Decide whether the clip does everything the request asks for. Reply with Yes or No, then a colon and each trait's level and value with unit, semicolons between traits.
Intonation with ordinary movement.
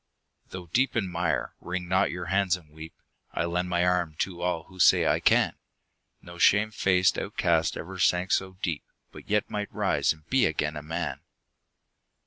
No: narrow, 2.2 semitones